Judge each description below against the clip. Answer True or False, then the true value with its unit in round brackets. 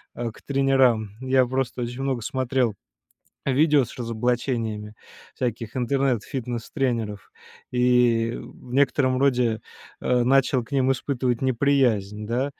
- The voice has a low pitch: True (125 Hz)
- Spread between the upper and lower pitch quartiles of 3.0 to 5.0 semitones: False (2.4 semitones)